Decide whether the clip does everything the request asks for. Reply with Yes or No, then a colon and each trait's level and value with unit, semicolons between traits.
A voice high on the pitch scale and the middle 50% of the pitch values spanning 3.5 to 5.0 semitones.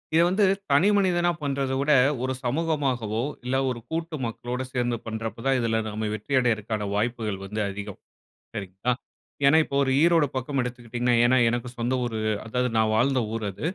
No: low, 125 Hz; average, 3.8 semitones